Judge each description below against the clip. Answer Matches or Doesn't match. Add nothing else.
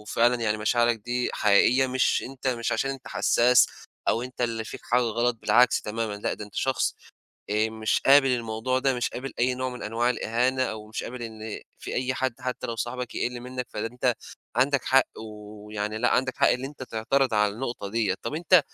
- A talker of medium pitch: Doesn't match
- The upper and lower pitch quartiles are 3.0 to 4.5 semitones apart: Doesn't match